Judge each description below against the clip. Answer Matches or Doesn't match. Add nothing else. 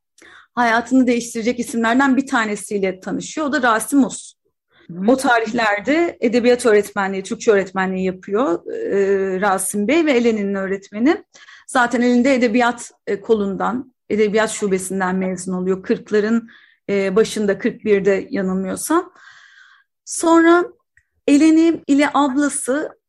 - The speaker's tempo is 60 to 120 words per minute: Matches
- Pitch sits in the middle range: Doesn't match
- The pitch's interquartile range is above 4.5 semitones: Matches